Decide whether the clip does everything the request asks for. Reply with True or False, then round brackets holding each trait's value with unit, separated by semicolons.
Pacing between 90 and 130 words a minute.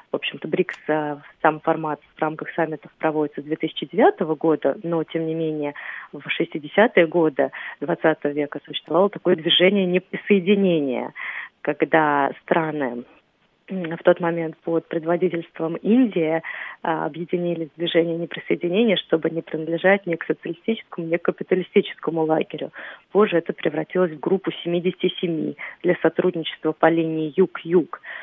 True (120 wpm)